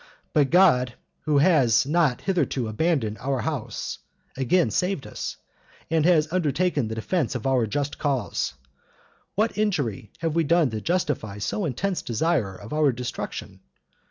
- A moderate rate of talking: Yes, average, 145 wpm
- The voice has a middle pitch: Yes, medium, 145 Hz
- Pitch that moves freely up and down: Yes, wide, 5.9 semitones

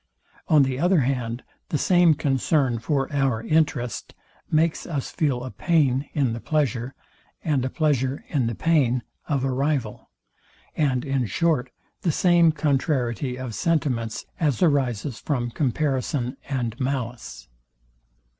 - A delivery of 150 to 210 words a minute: No, slow, 135 wpm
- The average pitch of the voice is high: No, low, 135 Hz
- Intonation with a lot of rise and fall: No, average, 3.7 semitones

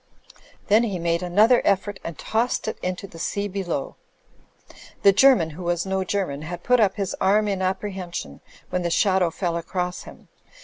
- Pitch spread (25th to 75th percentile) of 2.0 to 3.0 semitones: Yes, average, 2.7 semitones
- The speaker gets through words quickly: No, average, 175 wpm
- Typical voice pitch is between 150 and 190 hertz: Yes, medium, 185 Hz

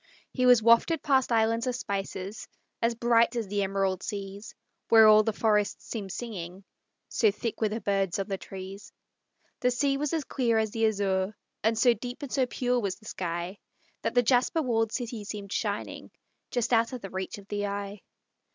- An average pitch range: Yes, average, 3.4 semitones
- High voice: Yes, high, 220 Hz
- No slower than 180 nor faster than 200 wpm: Yes, average, 190 wpm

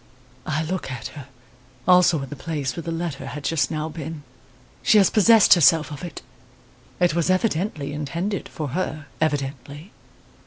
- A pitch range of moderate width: Yes, average, 3.4 semitones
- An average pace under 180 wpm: Yes, average, 160 wpm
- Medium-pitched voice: Yes, medium, 160 Hz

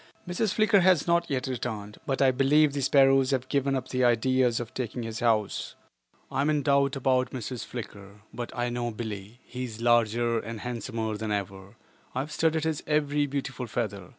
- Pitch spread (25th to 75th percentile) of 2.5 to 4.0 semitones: Yes, average, 3.5 semitones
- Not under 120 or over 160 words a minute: No, average, 190 wpm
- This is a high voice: No, low, 125 Hz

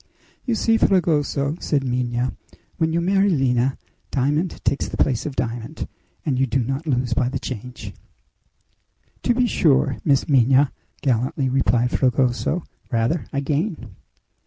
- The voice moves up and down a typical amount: Yes, average, 4.0 semitones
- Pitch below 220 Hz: Yes, low, 135 Hz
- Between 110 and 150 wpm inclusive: Yes, average, 140 wpm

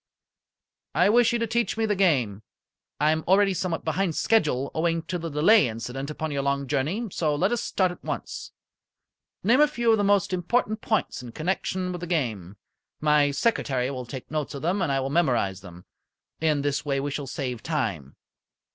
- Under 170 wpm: No, average, 195 wpm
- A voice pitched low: No, medium, 155 Hz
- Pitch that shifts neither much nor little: No, wide, 5.9 semitones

